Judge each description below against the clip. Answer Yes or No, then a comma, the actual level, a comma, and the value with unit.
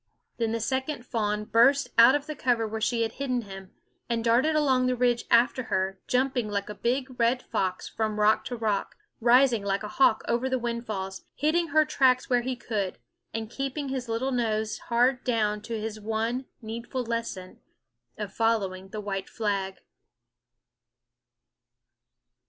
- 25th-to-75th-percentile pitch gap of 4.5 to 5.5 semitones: No, average, 3.1 semitones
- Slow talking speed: No, average, 165 wpm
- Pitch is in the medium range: No, high, 230 Hz